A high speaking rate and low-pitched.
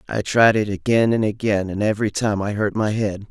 Yes: fast, 235 wpm; low, 105 Hz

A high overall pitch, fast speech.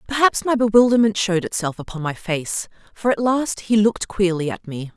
No: high, 205 Hz; average, 195 wpm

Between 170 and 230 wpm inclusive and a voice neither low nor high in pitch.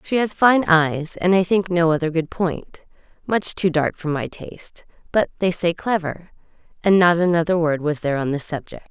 Yes: average, 180 wpm; medium, 170 Hz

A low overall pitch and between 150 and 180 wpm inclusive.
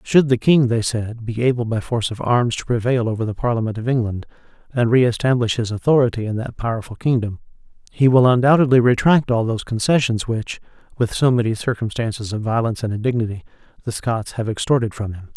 No: low, 115 Hz; average, 190 wpm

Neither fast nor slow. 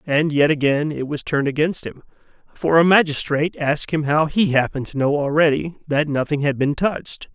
Yes: average, 195 wpm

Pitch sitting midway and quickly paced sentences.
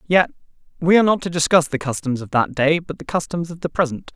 Yes: medium, 160 Hz; fast, 245 wpm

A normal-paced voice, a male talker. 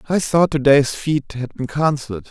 Yes: average, 180 wpm; male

